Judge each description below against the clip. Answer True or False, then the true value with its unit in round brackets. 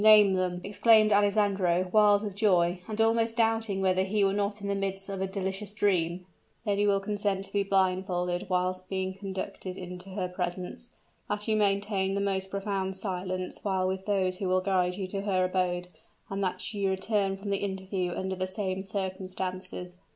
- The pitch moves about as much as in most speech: False (1.6 semitones)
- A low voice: False (195 Hz)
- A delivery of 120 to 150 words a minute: False (180 wpm)